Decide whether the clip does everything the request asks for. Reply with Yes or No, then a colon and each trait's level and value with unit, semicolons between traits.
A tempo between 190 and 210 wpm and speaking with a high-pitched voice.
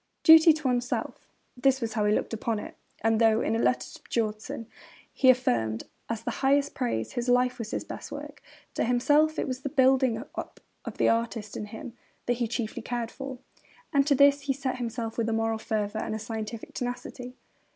Yes: fast, 205 wpm; high, 240 Hz